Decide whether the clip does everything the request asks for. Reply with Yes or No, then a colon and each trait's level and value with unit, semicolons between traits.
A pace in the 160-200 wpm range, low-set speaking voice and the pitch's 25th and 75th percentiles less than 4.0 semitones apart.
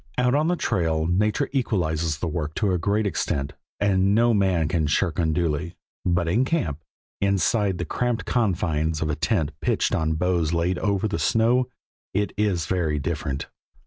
No: average, 170 wpm; very low, 90 Hz; average, 4.7 semitones